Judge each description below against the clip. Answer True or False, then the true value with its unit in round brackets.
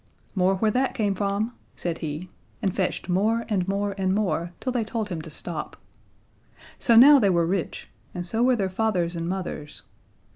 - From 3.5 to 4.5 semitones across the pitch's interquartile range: True (3.9 semitones)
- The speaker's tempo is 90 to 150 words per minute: False (185 wpm)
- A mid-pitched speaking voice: False (195 Hz)